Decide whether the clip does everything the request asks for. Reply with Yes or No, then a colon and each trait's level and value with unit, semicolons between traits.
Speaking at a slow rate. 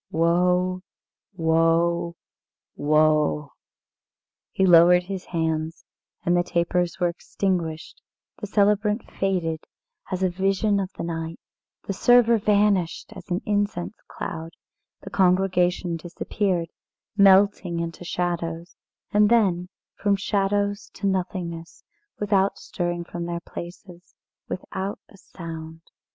Yes: slow, 110 wpm